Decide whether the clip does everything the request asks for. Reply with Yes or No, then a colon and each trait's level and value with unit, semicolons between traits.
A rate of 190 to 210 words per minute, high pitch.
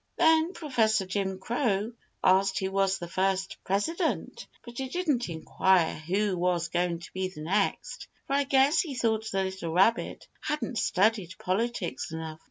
No: average, 160 wpm; high, 195 Hz